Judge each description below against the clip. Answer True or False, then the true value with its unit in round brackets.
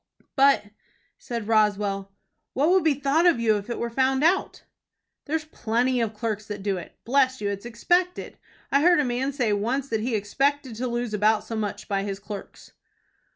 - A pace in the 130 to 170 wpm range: False (190 wpm)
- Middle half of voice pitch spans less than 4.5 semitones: False (4.8 semitones)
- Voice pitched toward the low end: False (235 Hz)